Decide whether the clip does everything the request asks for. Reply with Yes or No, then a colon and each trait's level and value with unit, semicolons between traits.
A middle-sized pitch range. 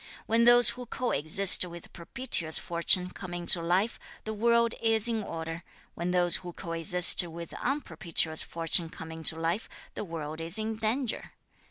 Yes: average, 5.0 semitones